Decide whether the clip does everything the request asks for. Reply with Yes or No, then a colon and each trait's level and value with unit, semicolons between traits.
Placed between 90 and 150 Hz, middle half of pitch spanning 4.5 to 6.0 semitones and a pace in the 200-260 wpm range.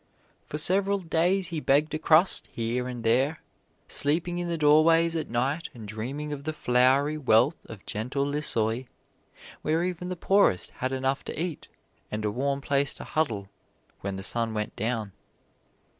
No: medium, 140 Hz; wide, 5.4 semitones; average, 165 wpm